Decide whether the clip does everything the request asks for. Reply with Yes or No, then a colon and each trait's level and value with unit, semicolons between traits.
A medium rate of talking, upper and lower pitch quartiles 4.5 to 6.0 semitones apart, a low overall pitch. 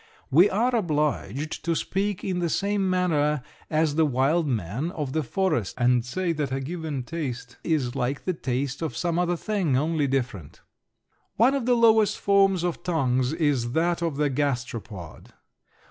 No: average, 165 wpm; average, 5.3 semitones; medium, 155 Hz